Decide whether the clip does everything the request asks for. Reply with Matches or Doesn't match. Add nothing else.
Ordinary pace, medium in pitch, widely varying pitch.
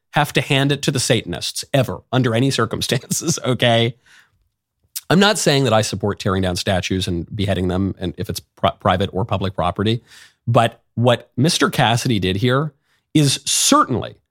Doesn't match